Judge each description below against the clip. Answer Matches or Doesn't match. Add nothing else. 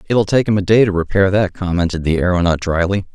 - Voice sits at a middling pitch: Doesn't match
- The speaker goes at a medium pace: Doesn't match